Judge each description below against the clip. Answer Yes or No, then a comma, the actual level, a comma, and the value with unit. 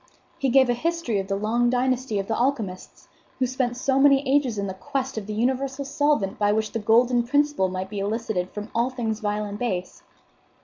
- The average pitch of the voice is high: Yes, high, 235 Hz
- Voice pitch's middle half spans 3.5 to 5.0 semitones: Yes, average, 4.2 semitones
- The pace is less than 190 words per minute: No, fast, 205 wpm